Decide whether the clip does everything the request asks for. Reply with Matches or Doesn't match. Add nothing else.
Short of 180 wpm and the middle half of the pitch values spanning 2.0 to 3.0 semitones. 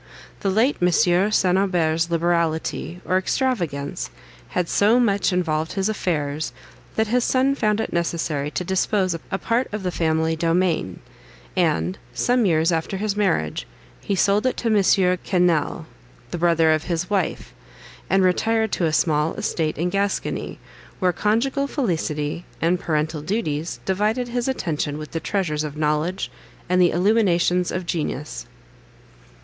Doesn't match